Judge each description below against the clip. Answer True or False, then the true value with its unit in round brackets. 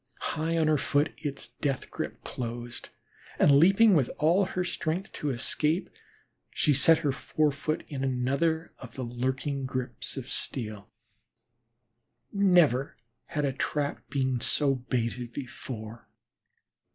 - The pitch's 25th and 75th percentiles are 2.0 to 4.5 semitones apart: True (3.7 semitones)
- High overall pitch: False (140 Hz)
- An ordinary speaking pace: False (130 wpm)